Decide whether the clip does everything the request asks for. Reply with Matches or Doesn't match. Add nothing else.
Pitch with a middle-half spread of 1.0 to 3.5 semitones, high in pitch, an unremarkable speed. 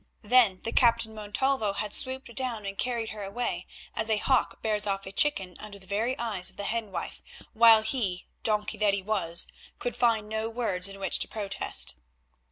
Matches